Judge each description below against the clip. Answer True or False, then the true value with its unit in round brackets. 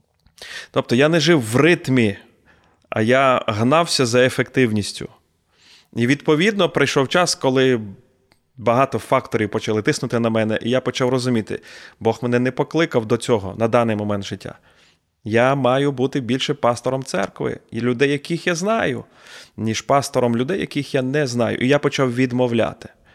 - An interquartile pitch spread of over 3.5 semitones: True (4.0 semitones)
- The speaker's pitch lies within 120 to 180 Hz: True (125 Hz)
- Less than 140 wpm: False (150 wpm)